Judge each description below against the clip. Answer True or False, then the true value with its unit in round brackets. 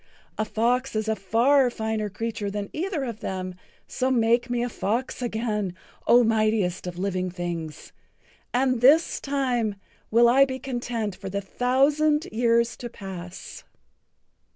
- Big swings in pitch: False (3.8 semitones)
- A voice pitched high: True (230 Hz)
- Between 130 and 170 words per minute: True (145 wpm)